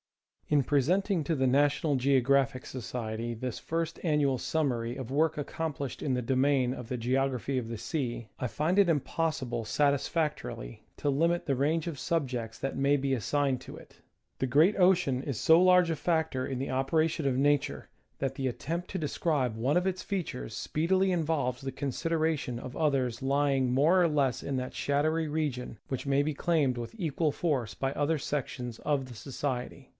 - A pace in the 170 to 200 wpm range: Yes, average, 180 wpm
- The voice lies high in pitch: No, medium, 140 Hz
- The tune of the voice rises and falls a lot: No, average, 3.8 semitones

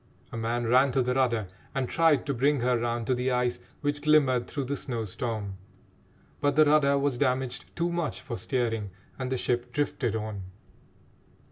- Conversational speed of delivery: Yes, average, 180 wpm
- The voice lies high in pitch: No, low, 125 Hz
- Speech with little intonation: No, average, 3.1 semitones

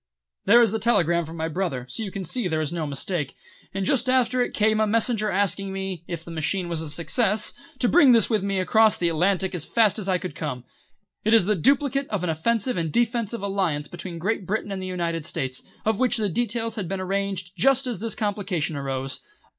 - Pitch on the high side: Yes, high, 195 Hz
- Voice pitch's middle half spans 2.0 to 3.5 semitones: No, average, 4.8 semitones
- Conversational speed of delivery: No, fast, 220 wpm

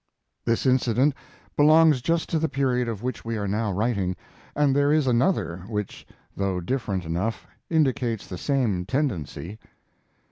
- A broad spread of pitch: Yes, wide, 5.8 semitones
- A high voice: No, low, 120 Hz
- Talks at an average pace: Yes, average, 150 wpm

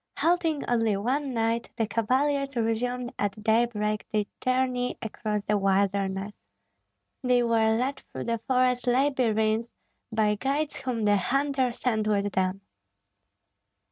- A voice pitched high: Yes, high, 230 Hz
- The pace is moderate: No, slow, 125 wpm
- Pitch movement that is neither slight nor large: Yes, average, 3.2 semitones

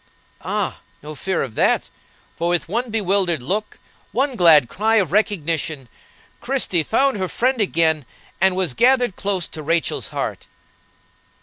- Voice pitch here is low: No, medium, 185 Hz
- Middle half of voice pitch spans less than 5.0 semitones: No, wide, 5.5 semitones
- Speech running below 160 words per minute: Yes, average, 140 wpm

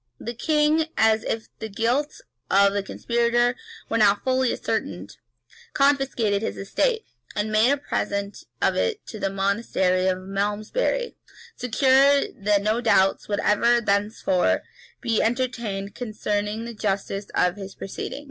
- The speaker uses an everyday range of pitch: Yes, average, 3.6 semitones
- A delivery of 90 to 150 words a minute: Yes, average, 140 wpm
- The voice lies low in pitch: No, high, 220 Hz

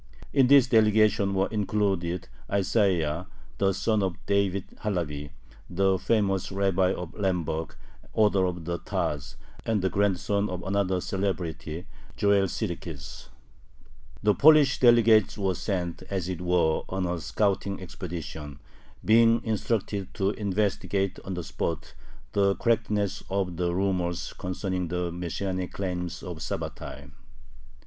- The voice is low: Yes, very low, 95 Hz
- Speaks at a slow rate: Yes, slow, 125 wpm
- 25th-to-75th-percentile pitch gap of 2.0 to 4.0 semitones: Yes, narrow, 2.5 semitones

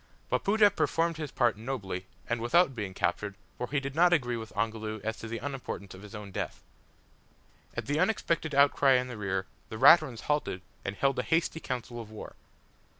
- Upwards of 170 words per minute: Yes, average, 190 wpm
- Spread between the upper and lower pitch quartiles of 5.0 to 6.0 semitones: Yes, average, 5.3 semitones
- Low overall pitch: Yes, low, 120 Hz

